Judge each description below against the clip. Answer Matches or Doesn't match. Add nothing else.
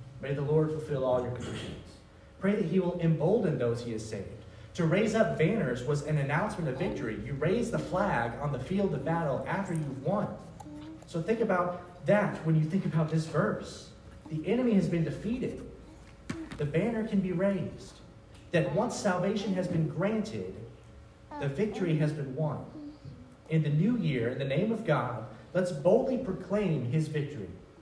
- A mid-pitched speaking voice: Matches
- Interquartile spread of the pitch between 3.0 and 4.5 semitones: Doesn't match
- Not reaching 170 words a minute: Doesn't match